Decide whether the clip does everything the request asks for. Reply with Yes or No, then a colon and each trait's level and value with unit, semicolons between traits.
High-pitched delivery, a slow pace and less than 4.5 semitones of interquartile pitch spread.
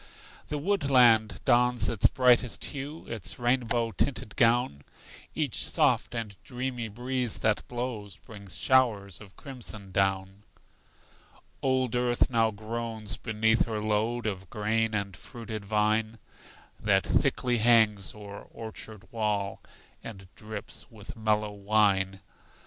No: low, 110 Hz; slow, 120 wpm; average, 2.8 semitones